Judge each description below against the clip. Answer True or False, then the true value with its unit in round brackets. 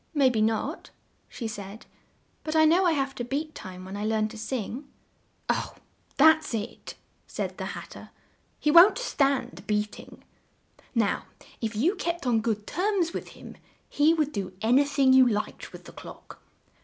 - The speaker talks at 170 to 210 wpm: True (180 wpm)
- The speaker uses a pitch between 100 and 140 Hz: False (260 Hz)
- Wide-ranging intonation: True (6.1 semitones)